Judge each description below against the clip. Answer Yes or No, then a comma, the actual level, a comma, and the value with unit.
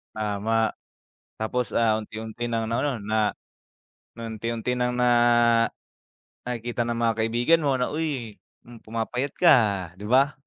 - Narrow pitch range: Yes, narrow, 1.9 semitones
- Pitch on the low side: Yes, low, 115 Hz